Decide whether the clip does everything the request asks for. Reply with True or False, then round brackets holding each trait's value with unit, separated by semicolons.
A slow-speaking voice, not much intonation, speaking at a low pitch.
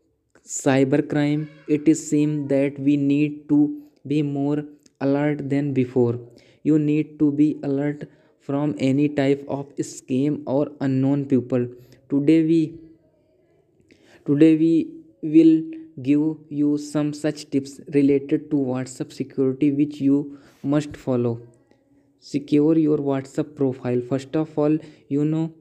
False (125 wpm; 1.7 semitones; 145 Hz)